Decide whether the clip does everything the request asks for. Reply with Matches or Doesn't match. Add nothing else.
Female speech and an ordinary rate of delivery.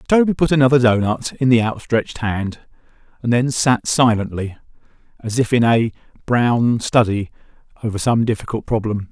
Doesn't match